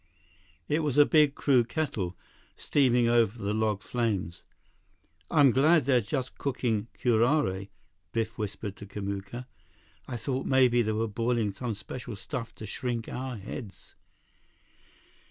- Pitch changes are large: No, average, 3.8 semitones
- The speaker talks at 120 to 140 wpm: Yes, slow, 135 wpm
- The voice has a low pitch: Yes, low, 120 Hz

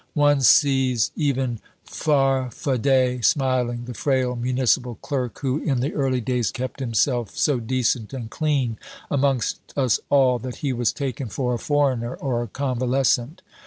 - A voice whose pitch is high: No, low, 130 Hz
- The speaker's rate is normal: Yes, average, 145 wpm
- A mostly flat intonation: Yes, narrow, 2.1 semitones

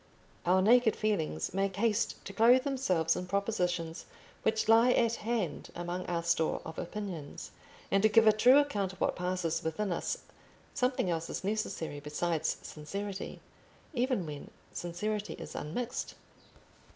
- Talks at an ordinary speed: Yes, average, 145 wpm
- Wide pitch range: No, average, 4.7 semitones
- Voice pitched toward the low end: No, high, 195 Hz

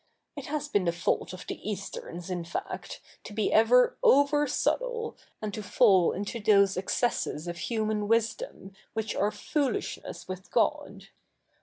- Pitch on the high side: Yes, high, 210 Hz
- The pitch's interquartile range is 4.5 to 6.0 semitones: Yes, average, 4.9 semitones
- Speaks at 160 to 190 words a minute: No, average, 150 wpm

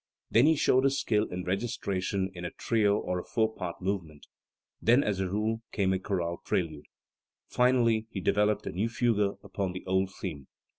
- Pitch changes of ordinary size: Yes, average, 3.4 semitones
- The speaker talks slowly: No, average, 185 wpm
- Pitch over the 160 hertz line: No, low, 100 Hz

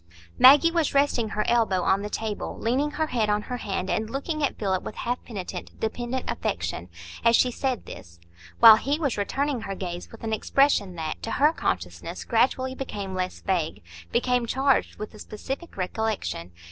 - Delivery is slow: No, average, 175 wpm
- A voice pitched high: Yes, high, 225 Hz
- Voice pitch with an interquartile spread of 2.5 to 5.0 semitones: No, wide, 5.5 semitones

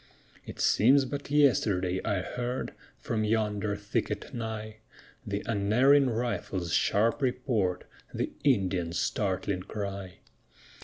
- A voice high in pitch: No, low, 105 Hz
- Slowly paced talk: Yes, slow, 105 wpm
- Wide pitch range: No, average, 4.0 semitones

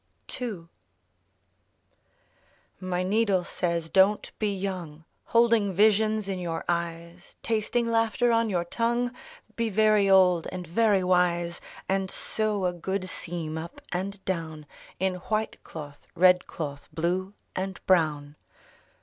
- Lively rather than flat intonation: No, average, 3.8 semitones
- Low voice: No, medium, 185 Hz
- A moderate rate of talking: No, slow, 125 wpm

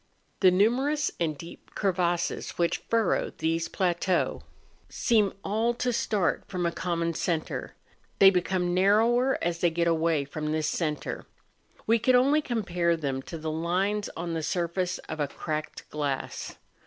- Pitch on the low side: No, medium, 175 Hz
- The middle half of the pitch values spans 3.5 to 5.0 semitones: Yes, average, 4.0 semitones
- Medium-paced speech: Yes, average, 150 wpm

